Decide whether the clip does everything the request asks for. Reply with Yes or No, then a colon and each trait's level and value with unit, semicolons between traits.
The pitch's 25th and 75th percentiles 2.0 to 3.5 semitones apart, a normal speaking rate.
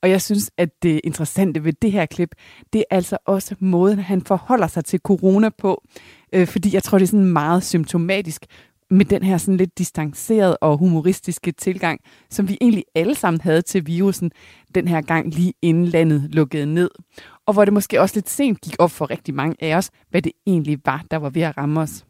Yes: average, 3.2 semitones; average, 210 wpm